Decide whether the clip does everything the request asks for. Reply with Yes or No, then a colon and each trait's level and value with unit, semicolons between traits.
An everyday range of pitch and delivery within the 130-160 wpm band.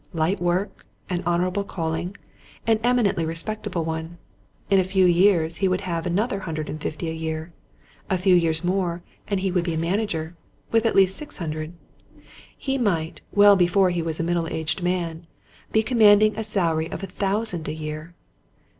No: average, 3.4 semitones; average, 180 wpm